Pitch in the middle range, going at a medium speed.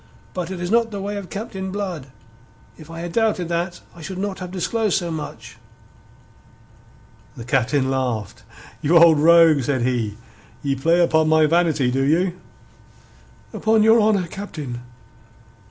Yes: medium, 170 Hz; average, 155 wpm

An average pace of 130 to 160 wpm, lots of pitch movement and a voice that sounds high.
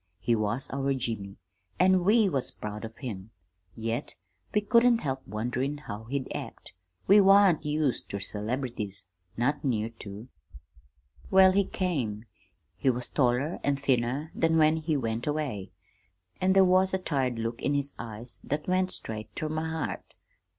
No: average, 155 wpm; wide, 6.0 semitones; low, 135 Hz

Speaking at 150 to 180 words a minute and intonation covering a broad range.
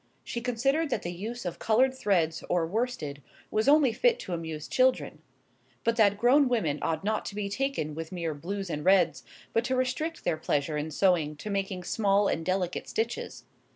No: average, 190 wpm; wide, 6.8 semitones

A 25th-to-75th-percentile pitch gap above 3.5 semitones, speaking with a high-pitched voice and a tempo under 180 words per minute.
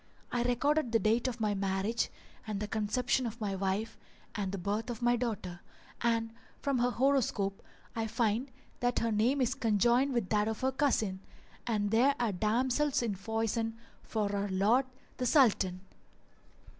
No: average, 3.2 semitones; high, 225 Hz; average, 170 wpm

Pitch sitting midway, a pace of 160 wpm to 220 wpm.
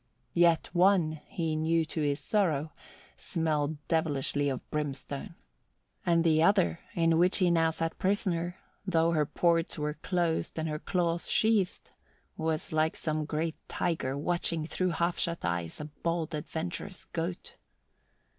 No: medium, 165 Hz; average, 145 wpm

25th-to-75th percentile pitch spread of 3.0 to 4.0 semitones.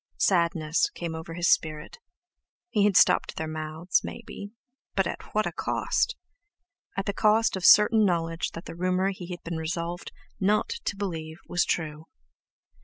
Yes: average, 3.3 semitones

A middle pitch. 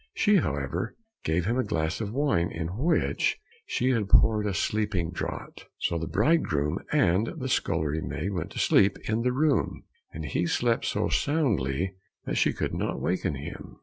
No: very low, 95 Hz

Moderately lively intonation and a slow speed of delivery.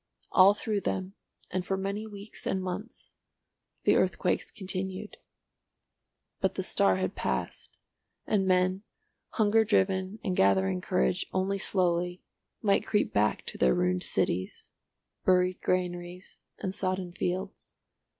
No: narrow, 2.0 semitones; slow, 125 wpm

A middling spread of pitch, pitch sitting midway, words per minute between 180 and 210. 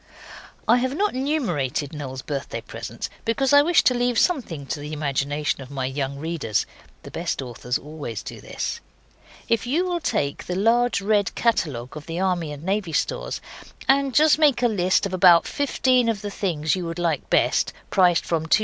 No: wide, 9.0 semitones; medium, 175 Hz; average, 185 wpm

